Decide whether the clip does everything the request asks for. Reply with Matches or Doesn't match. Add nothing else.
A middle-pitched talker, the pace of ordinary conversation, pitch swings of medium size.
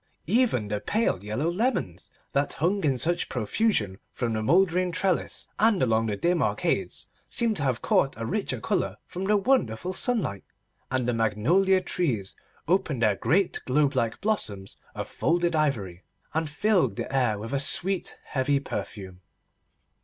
Doesn't match